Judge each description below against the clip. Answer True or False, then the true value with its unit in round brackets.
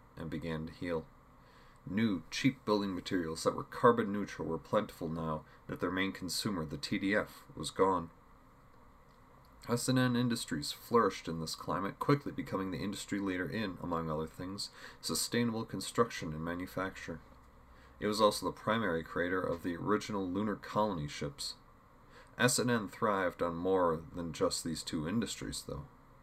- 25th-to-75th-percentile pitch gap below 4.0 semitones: False (4.5 semitones)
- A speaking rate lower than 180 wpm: True (155 wpm)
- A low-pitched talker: True (90 Hz)